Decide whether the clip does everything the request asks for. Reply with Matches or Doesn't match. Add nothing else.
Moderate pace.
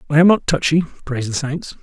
Doesn't match